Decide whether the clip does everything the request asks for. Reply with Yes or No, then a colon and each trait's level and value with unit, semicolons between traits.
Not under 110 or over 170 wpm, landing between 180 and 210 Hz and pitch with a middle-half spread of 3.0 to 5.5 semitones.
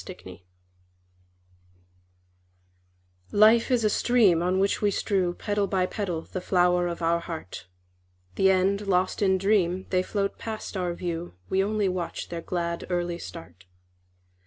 No: average, 140 wpm; medium, 185 Hz; narrow, 2.6 semitones